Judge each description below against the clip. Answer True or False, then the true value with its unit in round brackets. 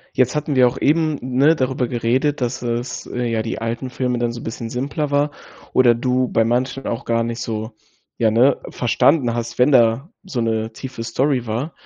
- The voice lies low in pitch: True (125 Hz)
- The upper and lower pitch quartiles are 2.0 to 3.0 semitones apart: True (2.5 semitones)